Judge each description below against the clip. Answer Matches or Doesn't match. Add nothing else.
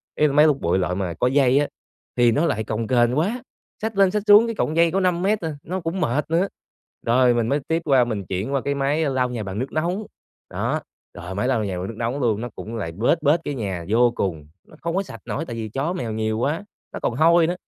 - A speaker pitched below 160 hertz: Matches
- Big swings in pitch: Matches